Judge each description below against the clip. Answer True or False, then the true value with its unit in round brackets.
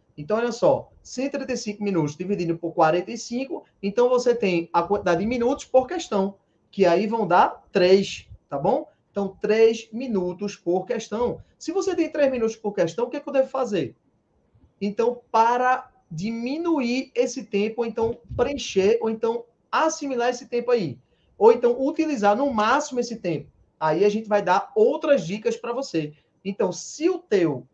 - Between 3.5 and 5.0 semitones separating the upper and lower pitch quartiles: True (4.7 semitones)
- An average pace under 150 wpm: False (165 wpm)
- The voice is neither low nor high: False (230 Hz)